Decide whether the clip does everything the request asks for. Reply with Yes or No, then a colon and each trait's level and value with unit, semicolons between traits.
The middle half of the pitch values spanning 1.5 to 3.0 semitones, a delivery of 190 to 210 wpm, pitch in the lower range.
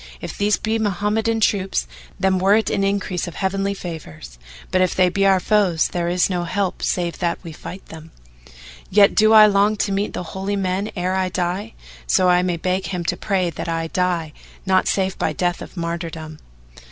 No: narrow, 2.4 semitones; average, 200 wpm; medium, 185 Hz